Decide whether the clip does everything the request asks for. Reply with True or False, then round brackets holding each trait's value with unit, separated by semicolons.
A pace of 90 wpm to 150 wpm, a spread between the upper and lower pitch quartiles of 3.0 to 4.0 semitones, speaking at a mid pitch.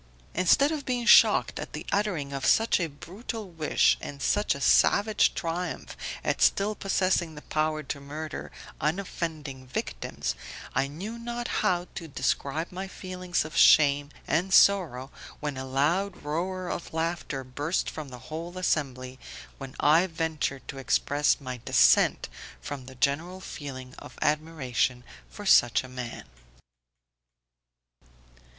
False (140 wpm; 5.1 semitones; 155 Hz)